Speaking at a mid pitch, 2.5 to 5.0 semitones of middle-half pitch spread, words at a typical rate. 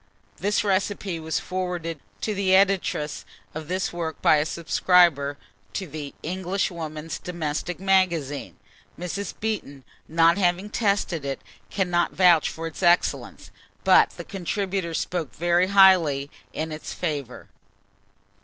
No: medium, 175 Hz; average, 3.2 semitones; slow, 125 wpm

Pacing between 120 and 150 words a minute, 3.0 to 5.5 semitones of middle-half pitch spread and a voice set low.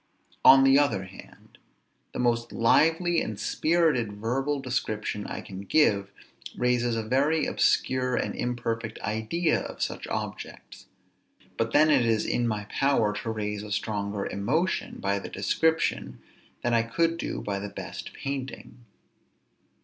Yes: average, 140 wpm; average, 4.9 semitones; low, 120 Hz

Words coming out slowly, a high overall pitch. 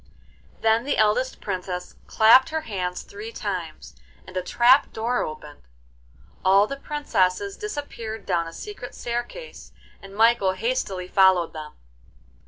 Yes: slow, 130 wpm; high, 210 Hz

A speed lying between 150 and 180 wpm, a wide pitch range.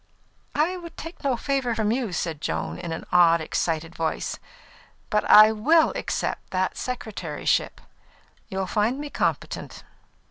No: average, 140 wpm; wide, 8.1 semitones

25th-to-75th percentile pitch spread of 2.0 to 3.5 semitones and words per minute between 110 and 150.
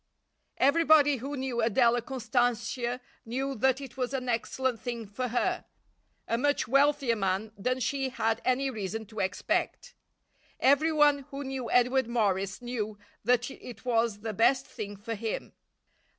Yes: average, 3.0 semitones; average, 145 wpm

